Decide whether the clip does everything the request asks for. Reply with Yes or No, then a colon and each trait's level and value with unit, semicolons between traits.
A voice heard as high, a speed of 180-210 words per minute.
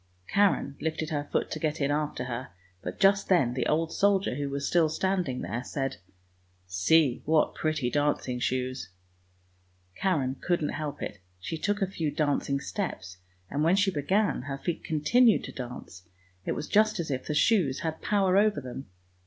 No: medium, 150 Hz; average, 185 wpm